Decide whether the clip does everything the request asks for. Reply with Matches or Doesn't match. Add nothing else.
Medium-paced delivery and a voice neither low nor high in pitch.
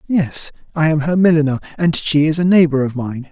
Doesn't match